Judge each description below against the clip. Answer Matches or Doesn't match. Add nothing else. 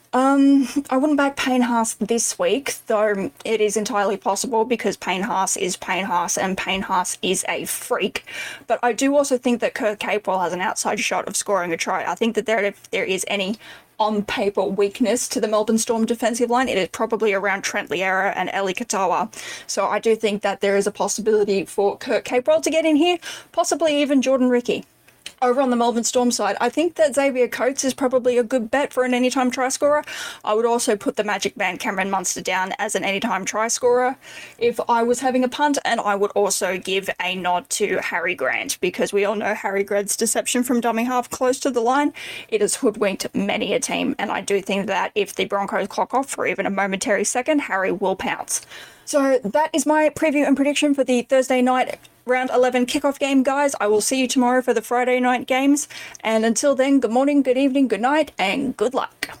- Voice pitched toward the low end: Doesn't match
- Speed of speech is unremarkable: Doesn't match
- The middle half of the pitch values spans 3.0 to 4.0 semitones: Doesn't match